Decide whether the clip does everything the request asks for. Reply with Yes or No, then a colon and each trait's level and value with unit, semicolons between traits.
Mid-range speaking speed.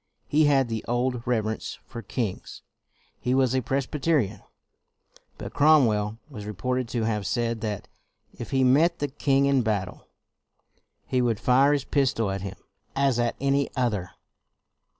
Yes: average, 150 wpm